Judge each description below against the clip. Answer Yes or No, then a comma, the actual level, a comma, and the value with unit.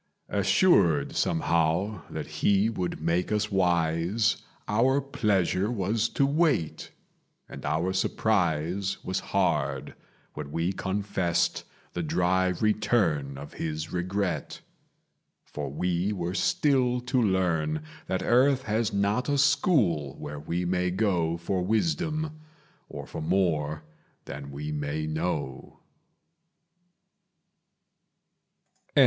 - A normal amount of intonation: Yes, average, 4.7 semitones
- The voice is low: Yes, very low, 95 Hz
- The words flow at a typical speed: No, slow, 105 wpm